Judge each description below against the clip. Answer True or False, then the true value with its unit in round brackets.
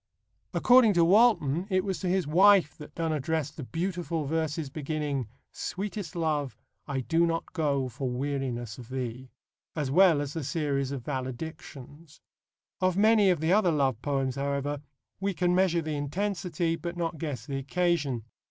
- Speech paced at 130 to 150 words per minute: False (160 wpm)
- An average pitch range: True (4.3 semitones)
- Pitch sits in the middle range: True (155 Hz)